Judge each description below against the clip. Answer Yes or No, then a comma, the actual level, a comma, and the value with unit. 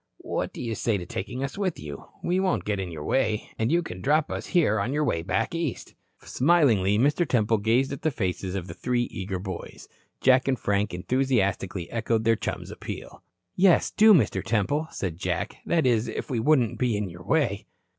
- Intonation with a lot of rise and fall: Yes, wide, 6.1 semitones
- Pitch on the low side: Yes, low, 115 Hz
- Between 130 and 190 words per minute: No, fast, 205 wpm